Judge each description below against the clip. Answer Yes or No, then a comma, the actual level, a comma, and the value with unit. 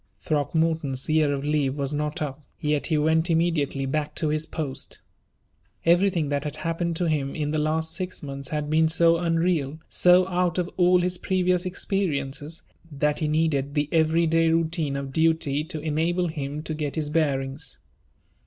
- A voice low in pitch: No, medium, 155 Hz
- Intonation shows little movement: Yes, narrow, 2.3 semitones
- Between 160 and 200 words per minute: Yes, average, 170 wpm